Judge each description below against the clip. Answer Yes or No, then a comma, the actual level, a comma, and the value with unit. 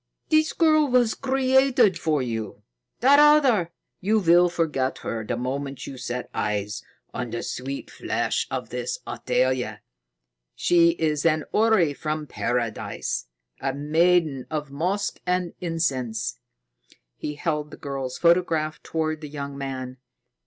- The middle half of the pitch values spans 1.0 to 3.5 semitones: No, average, 5.3 semitones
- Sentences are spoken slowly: Yes, slow, 130 wpm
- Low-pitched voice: No, medium, 155 Hz